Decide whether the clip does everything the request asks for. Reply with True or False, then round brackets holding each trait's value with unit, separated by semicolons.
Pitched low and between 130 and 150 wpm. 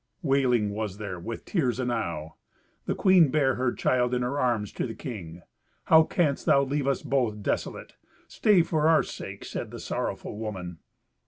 False (125 Hz; 170 wpm)